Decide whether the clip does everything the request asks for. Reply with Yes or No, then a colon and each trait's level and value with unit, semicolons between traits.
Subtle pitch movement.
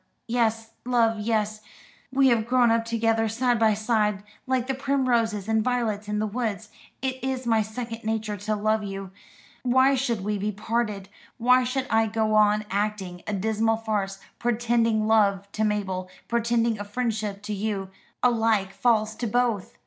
Yes: narrow, 2.2 semitones